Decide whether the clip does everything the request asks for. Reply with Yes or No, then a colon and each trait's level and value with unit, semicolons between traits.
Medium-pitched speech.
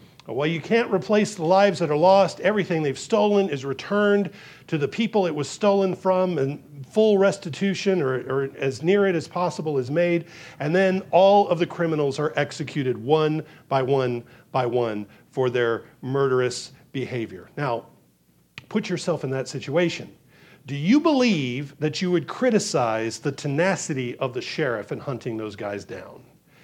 Yes: medium, 155 Hz